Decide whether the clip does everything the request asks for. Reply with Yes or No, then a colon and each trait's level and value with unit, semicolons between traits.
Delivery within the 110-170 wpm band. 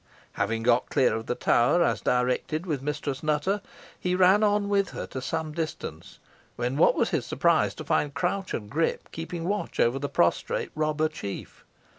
No: average, 180 wpm